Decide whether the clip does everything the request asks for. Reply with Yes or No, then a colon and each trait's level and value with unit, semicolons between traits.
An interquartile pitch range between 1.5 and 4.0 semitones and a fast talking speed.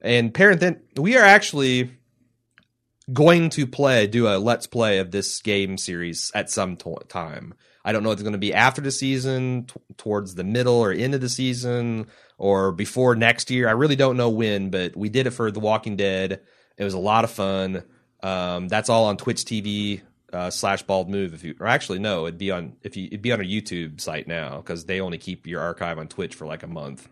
No: average, 4.5 semitones; fast, 225 wpm